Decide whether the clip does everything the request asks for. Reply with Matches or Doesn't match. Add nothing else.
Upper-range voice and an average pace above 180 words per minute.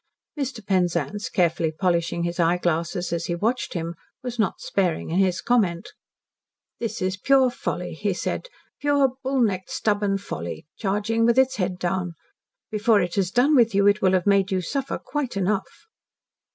Doesn't match